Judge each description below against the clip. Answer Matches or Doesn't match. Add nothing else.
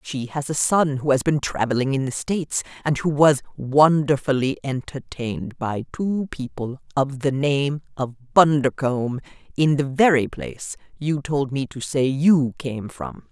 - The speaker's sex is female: Matches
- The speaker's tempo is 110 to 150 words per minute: Doesn't match